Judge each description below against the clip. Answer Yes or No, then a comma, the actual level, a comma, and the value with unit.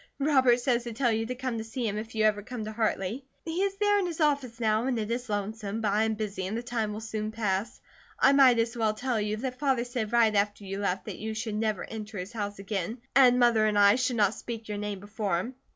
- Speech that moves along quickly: Yes, fast, 265 wpm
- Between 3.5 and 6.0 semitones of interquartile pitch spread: No, average, 2.8 semitones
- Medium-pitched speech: No, high, 220 Hz